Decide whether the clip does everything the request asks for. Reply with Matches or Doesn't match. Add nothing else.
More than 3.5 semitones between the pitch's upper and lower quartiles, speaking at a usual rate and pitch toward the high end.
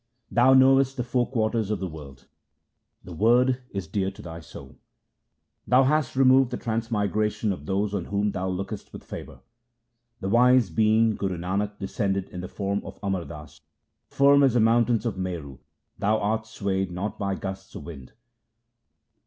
Doesn't match